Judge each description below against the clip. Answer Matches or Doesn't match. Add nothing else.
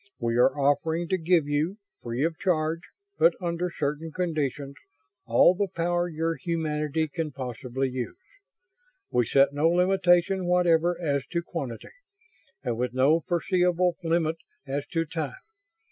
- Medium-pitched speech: Matches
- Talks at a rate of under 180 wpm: Matches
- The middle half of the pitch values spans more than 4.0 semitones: Doesn't match